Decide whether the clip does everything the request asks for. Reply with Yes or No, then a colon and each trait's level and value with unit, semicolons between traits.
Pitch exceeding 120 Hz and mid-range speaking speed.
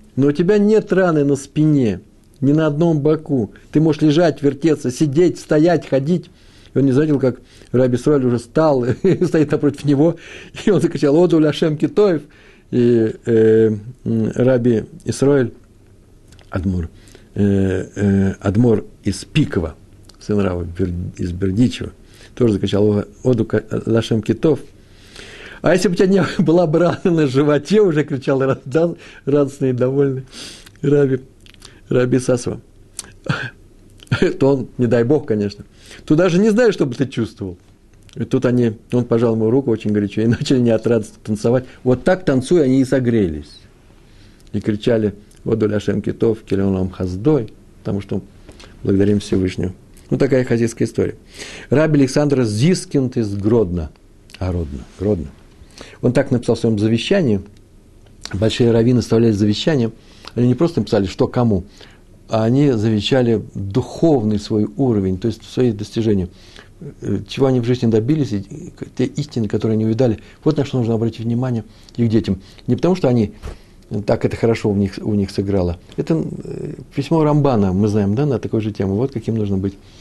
No: low, 115 Hz; average, 150 wpm